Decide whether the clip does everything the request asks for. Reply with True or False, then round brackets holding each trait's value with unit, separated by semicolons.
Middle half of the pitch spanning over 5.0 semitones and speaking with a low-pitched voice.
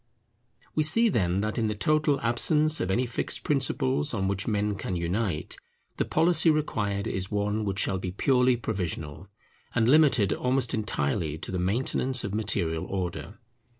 True (5.6 semitones; 105 Hz)